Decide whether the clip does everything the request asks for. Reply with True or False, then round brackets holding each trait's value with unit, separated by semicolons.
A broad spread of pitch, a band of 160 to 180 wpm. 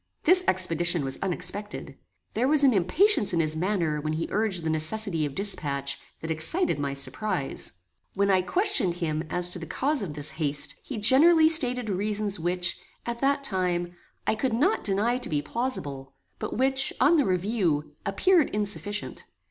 True (7.3 semitones; 170 wpm)